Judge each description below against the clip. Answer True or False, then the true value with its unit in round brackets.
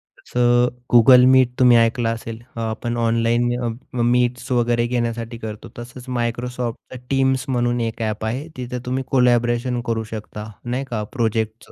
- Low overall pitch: True (120 Hz)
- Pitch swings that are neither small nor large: False (1.4 semitones)